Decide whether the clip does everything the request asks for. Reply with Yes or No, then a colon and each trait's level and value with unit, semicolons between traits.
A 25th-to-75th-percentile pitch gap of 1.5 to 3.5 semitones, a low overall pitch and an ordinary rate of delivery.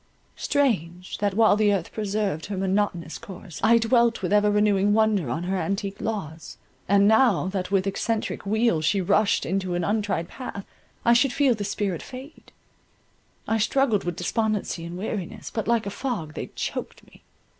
No: average, 3.0 semitones; high, 205 Hz; average, 170 wpm